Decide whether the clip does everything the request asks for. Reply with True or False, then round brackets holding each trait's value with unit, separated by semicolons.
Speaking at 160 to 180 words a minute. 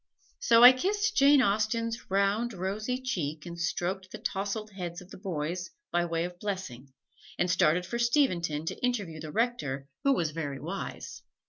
True (165 wpm)